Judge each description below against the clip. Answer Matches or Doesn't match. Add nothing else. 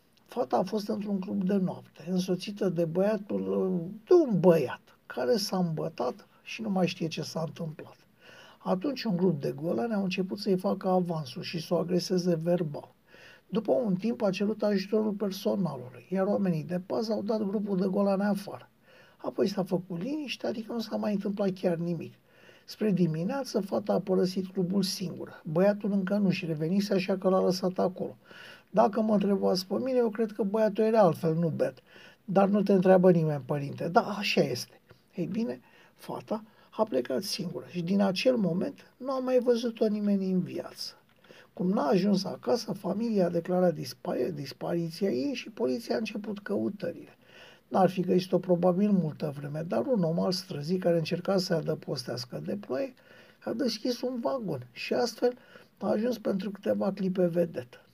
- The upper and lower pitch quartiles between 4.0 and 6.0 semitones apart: Doesn't match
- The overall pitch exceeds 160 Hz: Matches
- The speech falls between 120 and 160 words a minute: Doesn't match